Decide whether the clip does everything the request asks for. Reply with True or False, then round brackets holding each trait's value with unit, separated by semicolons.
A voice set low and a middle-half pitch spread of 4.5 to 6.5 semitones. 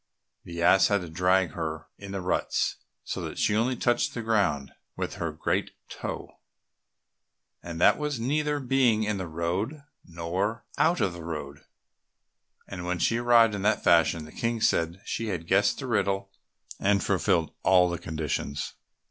True (95 Hz; 5.1 semitones)